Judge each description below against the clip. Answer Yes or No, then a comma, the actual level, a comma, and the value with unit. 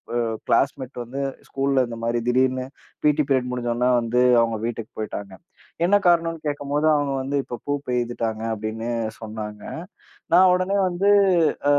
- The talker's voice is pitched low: Yes, low, 125 Hz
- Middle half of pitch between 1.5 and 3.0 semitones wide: No, average, 3.7 semitones